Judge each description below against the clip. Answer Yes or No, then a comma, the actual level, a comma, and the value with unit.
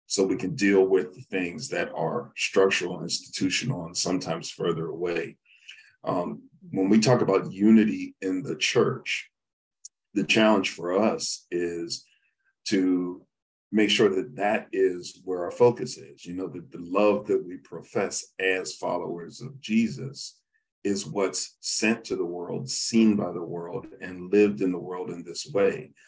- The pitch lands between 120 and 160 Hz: No, very low, 95 Hz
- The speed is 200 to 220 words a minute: No, average, 160 wpm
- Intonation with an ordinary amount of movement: Yes, average, 3.2 semitones